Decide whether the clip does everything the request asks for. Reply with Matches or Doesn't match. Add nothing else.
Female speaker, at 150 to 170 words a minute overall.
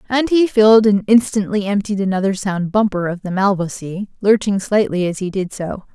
Doesn't match